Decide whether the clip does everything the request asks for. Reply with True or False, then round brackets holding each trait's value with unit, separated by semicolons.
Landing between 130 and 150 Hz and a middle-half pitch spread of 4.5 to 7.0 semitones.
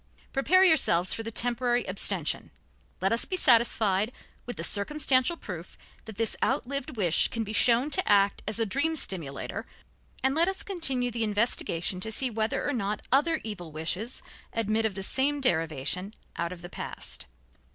False (225 Hz; 5.4 semitones)